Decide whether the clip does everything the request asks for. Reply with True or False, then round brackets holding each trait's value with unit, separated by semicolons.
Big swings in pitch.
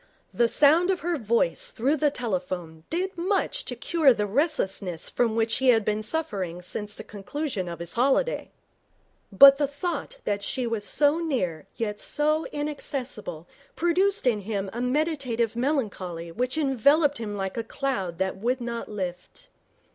True (6.6 semitones)